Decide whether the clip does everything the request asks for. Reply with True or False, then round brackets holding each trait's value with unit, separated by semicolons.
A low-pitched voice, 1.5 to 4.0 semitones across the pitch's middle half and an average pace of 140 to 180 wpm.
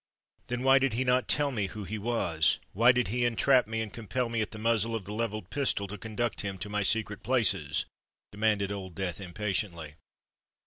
False (110 Hz; 3.3 semitones; 195 wpm)